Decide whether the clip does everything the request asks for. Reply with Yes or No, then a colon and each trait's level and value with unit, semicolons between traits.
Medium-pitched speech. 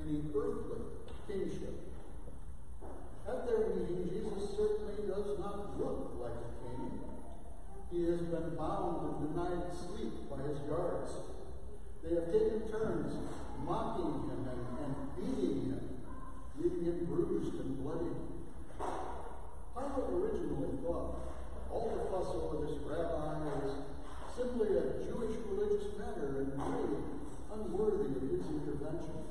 Yes: medium, 175 Hz